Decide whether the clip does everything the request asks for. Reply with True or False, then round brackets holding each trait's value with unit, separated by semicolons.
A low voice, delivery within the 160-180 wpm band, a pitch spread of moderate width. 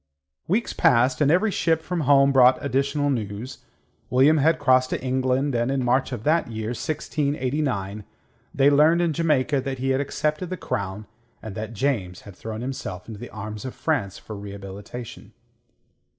True (130 Hz; 165 wpm; 4.8 semitones)